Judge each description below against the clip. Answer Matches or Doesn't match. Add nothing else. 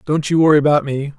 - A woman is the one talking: Doesn't match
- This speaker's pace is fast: Matches